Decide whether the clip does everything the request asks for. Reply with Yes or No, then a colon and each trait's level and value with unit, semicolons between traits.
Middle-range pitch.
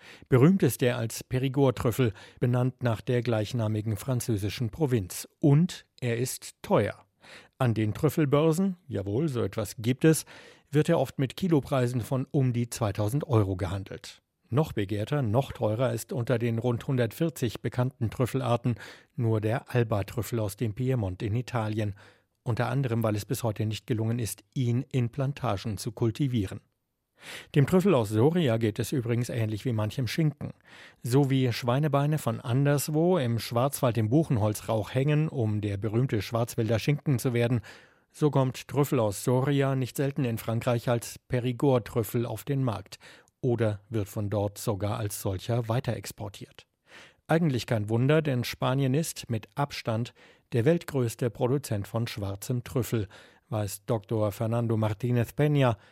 No: low, 120 Hz